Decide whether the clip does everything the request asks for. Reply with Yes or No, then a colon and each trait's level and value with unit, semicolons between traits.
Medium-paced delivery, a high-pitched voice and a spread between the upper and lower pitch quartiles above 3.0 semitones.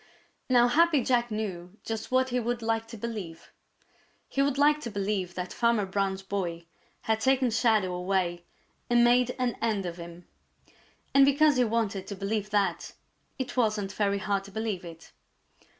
Yes: average, 165 wpm; high, 220 Hz; average, 4.0 semitones